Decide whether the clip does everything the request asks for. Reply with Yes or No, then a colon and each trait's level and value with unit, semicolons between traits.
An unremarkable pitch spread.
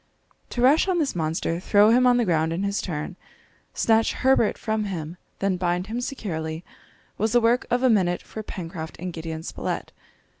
No: wide, 5.9 semitones